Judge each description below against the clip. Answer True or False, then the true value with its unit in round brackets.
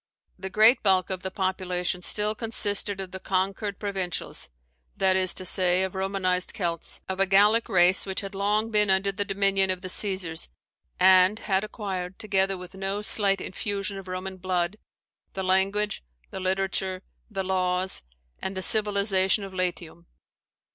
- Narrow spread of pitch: True (1.4 semitones)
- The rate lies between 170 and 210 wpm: False (160 wpm)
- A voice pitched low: False (190 Hz)